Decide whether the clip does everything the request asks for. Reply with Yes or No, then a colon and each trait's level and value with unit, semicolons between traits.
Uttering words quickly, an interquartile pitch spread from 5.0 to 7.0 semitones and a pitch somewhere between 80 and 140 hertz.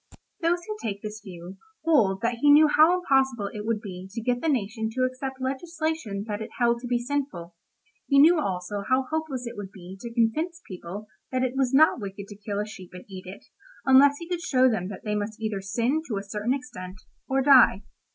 No: fast, 220 wpm; average, 5.3 semitones; high, 235 Hz